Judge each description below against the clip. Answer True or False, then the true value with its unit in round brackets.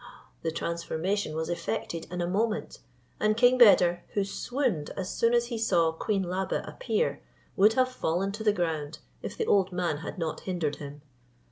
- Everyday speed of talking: True (175 wpm)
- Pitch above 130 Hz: True (185 Hz)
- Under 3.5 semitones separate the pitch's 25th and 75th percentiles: False (4.7 semitones)